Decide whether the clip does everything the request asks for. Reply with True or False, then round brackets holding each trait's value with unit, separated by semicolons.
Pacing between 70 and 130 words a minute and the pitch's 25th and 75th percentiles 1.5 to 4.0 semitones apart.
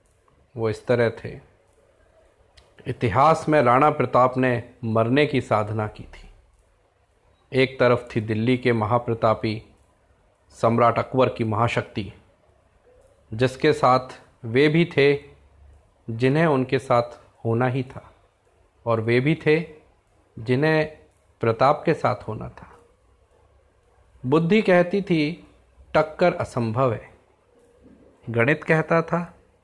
False (110 wpm; 4.5 semitones)